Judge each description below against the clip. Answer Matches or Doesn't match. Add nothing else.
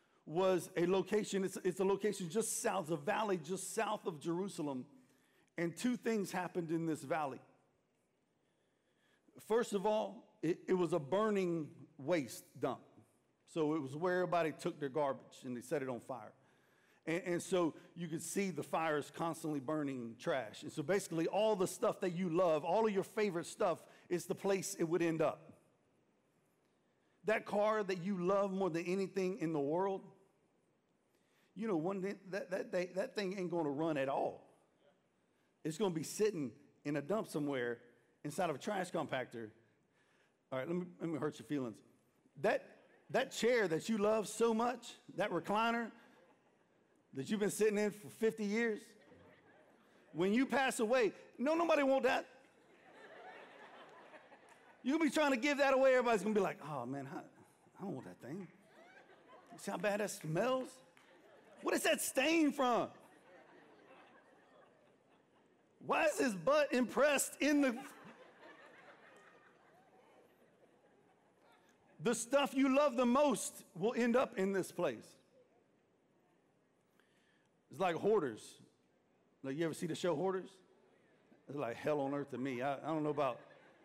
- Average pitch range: Doesn't match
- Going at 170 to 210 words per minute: Doesn't match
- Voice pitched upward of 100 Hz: Matches